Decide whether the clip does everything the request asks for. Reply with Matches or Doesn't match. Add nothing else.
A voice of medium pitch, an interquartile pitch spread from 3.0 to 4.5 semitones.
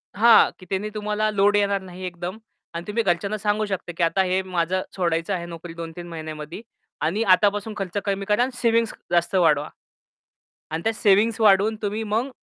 Doesn't match